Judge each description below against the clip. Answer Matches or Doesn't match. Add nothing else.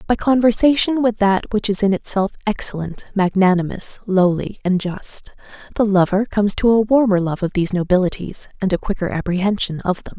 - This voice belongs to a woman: Matches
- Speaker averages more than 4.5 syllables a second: Matches